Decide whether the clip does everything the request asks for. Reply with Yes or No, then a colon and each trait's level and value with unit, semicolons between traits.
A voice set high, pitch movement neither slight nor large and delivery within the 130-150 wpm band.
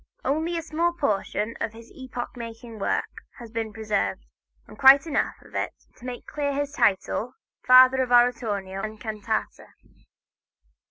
Yes: high, 240 Hz; average, 4.0 semitones; average, 140 wpm